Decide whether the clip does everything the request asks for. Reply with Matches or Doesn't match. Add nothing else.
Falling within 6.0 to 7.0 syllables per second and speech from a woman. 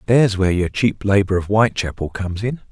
Doesn't match